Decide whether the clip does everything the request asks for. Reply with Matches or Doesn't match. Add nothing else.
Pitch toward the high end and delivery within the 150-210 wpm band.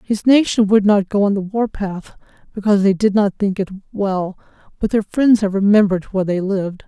Matches